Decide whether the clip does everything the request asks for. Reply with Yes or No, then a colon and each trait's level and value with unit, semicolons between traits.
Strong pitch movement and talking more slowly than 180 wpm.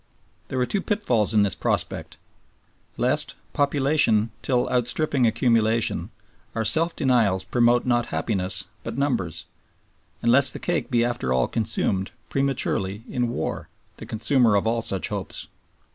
No: average, 3.8 semitones; average, 140 wpm